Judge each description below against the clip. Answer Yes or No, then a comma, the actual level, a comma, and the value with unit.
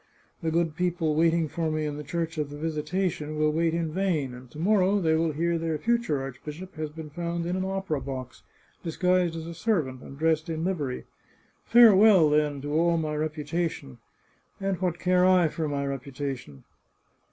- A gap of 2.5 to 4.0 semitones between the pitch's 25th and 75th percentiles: Yes, average, 2.8 semitones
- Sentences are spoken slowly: No, average, 185 wpm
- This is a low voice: No, medium, 160 Hz